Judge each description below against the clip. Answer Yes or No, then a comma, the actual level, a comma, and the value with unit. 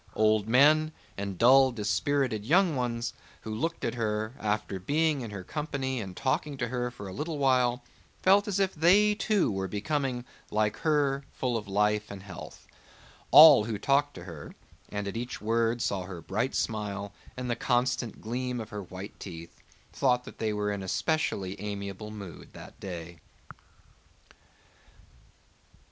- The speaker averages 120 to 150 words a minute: No, average, 160 wpm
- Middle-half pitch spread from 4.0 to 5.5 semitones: Yes, average, 5.1 semitones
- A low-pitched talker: Yes, low, 115 Hz